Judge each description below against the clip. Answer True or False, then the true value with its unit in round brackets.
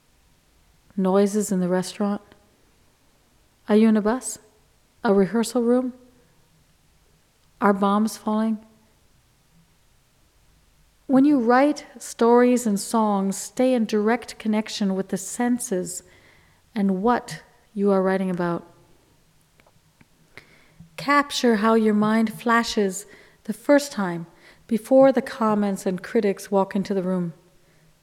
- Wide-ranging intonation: False (3.7 semitones)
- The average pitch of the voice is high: True (210 Hz)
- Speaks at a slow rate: True (110 wpm)